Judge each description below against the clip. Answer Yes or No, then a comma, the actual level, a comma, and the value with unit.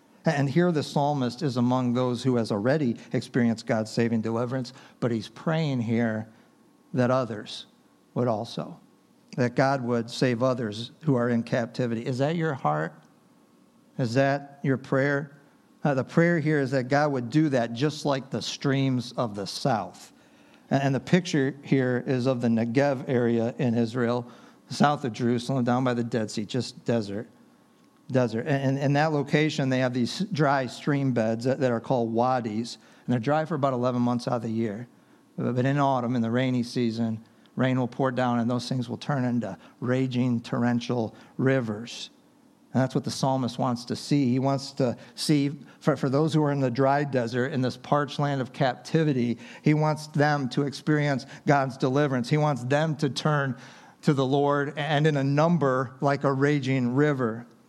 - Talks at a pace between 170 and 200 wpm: Yes, average, 180 wpm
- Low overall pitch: Yes, low, 130 Hz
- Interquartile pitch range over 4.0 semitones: No, average, 2.9 semitones